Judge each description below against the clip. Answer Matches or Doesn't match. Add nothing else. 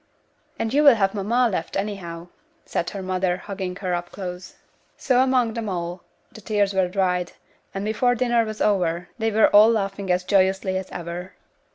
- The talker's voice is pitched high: Matches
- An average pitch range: Matches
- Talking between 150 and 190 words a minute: Matches